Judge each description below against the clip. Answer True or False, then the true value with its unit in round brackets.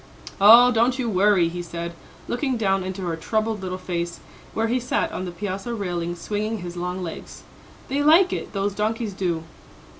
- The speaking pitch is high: True (195 Hz)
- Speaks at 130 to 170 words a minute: False (180 wpm)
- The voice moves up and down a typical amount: True (4.1 semitones)